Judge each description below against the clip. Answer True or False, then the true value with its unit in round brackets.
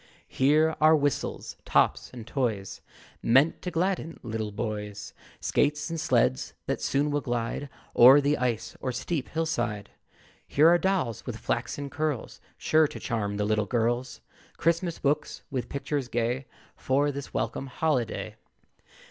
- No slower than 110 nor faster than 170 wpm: True (145 wpm)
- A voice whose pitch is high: False (135 Hz)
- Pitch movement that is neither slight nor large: True (4.8 semitones)